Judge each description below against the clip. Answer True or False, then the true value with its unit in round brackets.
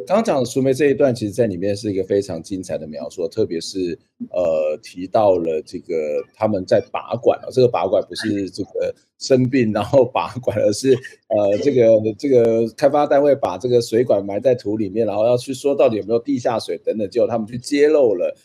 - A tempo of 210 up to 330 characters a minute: True (310 characters per minute)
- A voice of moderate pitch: False (125 Hz)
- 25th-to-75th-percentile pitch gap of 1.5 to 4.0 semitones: False (5.2 semitones)